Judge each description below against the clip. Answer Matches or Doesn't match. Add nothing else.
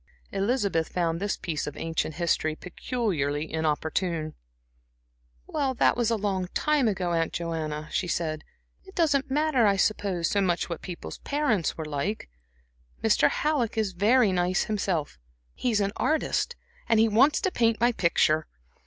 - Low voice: Doesn't match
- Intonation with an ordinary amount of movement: Doesn't match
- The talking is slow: Doesn't match